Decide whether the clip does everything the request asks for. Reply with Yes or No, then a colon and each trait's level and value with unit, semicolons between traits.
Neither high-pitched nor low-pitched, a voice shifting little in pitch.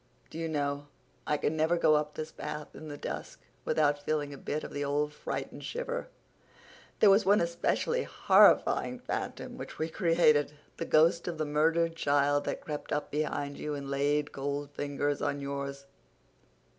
Yes: medium, 150 Hz; narrow, 1.9 semitones